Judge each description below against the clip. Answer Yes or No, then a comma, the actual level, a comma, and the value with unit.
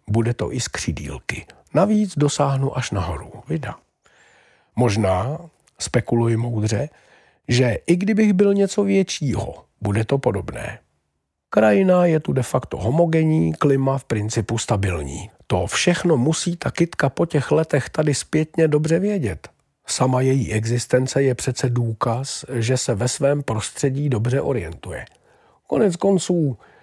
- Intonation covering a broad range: Yes, wide, 5.8 semitones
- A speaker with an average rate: Yes, average, 130 wpm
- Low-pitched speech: Yes, low, 130 Hz